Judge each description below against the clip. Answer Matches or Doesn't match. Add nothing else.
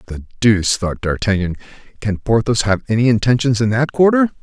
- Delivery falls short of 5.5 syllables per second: Doesn't match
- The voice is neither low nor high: Doesn't match